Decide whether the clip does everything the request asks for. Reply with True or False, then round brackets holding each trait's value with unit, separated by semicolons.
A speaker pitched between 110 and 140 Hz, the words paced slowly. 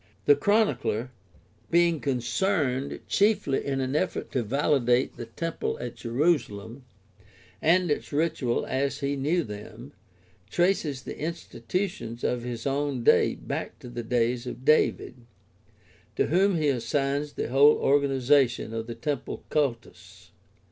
True (135 Hz; 130 wpm)